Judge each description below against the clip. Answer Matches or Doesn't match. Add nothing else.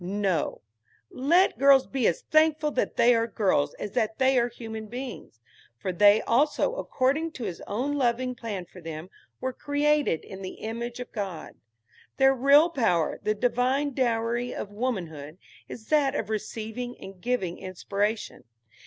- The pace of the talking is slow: Doesn't match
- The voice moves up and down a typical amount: Matches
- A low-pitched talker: Doesn't match